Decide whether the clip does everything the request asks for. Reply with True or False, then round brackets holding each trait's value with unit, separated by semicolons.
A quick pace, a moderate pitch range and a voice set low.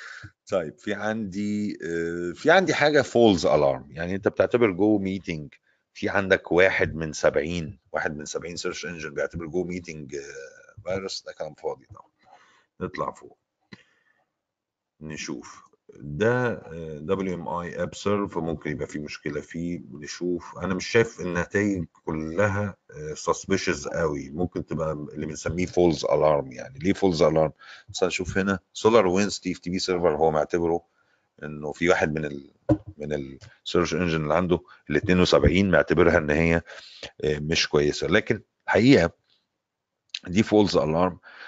True (140 wpm; 4.2 semitones; 90 Hz)